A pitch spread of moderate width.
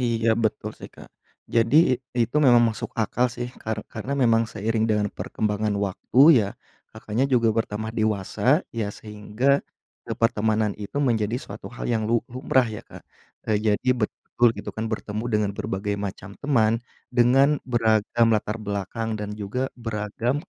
No: narrow, 2.0 semitones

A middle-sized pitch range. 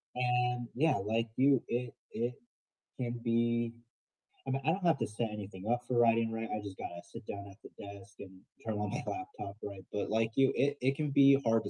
Yes: average, 3.5 semitones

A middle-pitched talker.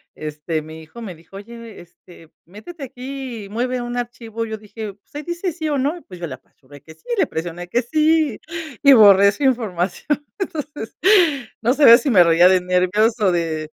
No: high, 220 Hz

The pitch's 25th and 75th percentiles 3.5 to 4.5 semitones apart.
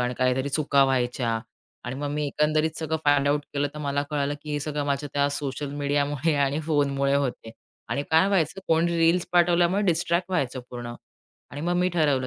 No: narrow, 2.6 semitones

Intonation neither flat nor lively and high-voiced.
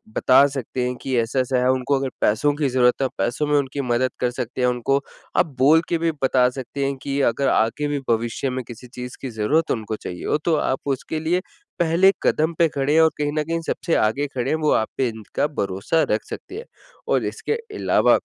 No: average, 3.3 semitones; low, 135 Hz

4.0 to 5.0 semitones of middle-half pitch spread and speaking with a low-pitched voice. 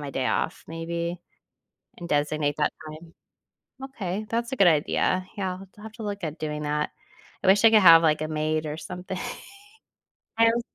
No: average, 4.5 semitones; medium, 170 Hz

